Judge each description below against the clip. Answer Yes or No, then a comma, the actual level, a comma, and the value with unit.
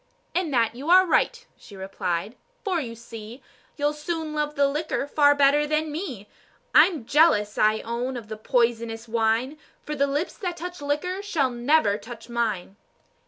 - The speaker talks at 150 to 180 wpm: Yes, average, 165 wpm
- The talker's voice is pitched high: Yes, very high, 275 Hz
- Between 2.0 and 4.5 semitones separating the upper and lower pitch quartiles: No, average, 5.2 semitones